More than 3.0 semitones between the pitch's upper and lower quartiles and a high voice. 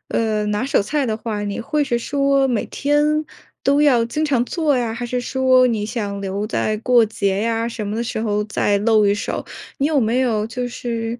Yes: average, 3.6 semitones; high, 235 Hz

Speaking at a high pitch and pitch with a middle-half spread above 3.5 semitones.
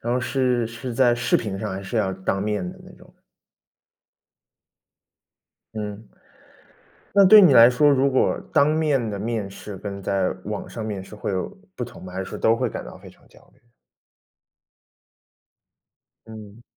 No: low, 110 Hz; average, 4.0 semitones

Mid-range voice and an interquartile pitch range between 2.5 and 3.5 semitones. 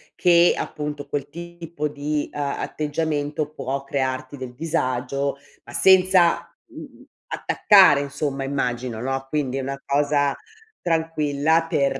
Yes: medium, 145 Hz; average, 2.8 semitones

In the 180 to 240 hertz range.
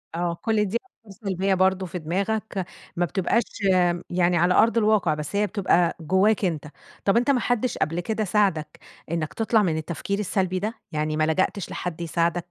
Yes: medium, 185 Hz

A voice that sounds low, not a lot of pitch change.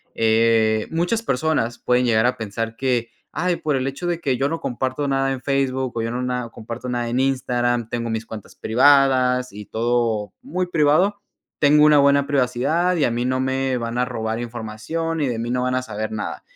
No: low, 125 Hz; average, 3.3 semitones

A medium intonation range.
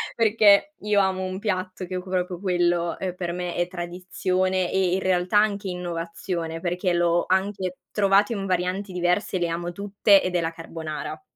No: narrow, 1.9 semitones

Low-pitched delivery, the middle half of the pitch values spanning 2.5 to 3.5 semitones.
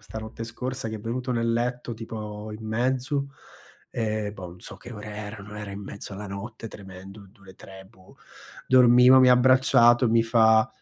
Yes: low, 110 Hz; average, 2.9 semitones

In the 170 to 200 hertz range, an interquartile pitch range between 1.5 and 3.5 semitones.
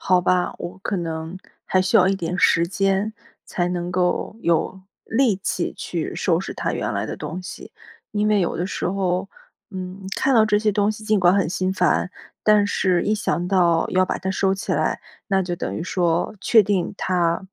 Yes: medium, 185 Hz; narrow, 2.4 semitones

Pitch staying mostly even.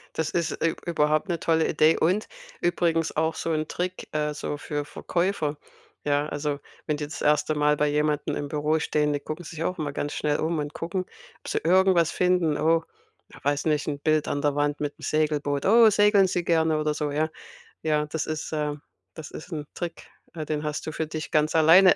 Yes: narrow, 1.9 semitones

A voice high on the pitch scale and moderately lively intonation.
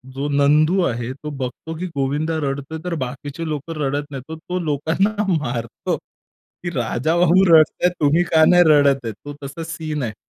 No: medium, 150 Hz; average, 3.1 semitones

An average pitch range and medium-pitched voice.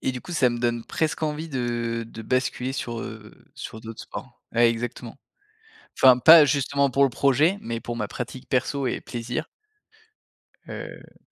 No: average, 3.0 semitones; low, 125 Hz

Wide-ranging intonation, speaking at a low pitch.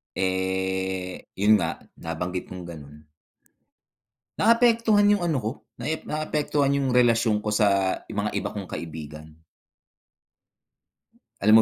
Yes: wide, 7.4 semitones; low, 100 Hz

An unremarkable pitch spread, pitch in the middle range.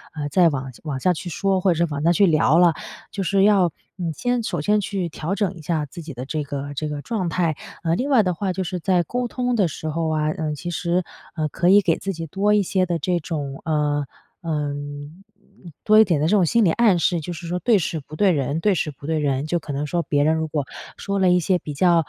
Yes: average, 3.9 semitones; medium, 170 Hz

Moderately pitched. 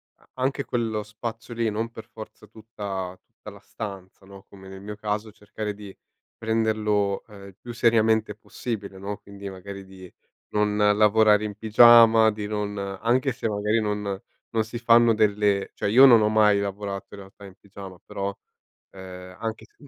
No: low, 105 Hz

